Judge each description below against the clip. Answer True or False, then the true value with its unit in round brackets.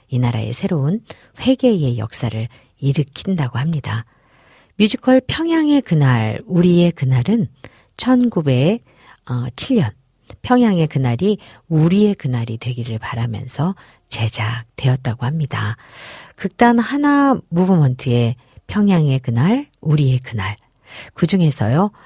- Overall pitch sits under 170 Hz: True (140 Hz)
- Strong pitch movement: True (8.1 semitones)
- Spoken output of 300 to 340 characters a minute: False (240 characters per minute)